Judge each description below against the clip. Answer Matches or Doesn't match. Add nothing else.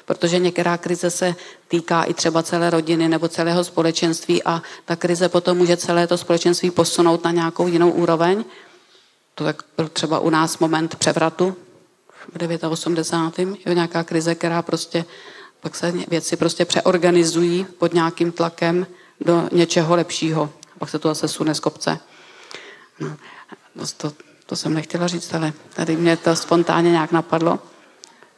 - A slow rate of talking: Doesn't match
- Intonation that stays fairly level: Matches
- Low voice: Doesn't match